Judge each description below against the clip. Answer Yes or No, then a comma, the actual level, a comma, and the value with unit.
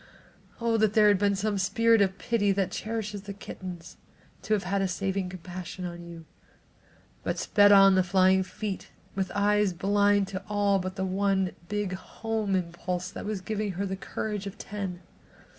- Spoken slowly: No, average, 175 wpm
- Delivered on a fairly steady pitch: Yes, narrow, 1.8 semitones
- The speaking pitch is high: Yes, high, 195 Hz